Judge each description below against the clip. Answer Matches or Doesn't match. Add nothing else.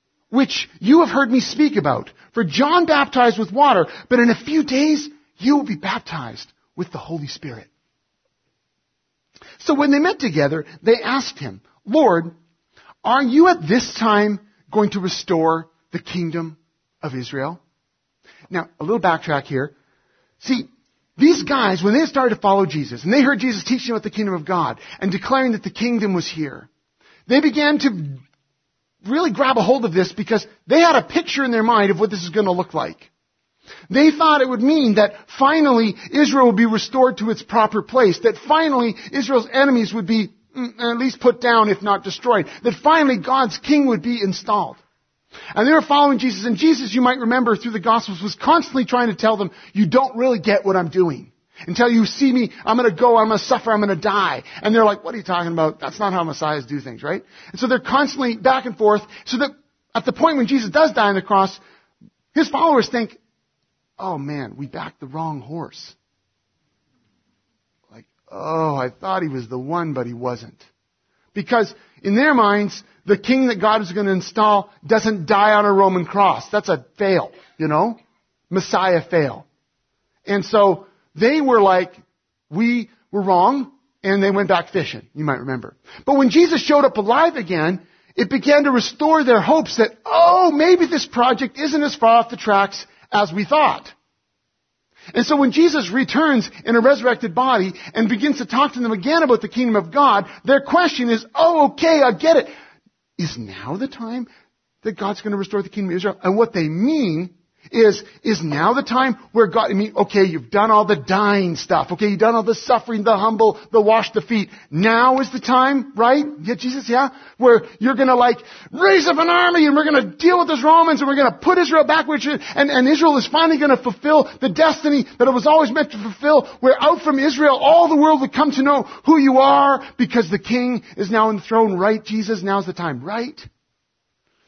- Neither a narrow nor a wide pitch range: Doesn't match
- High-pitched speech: Matches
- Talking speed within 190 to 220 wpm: Matches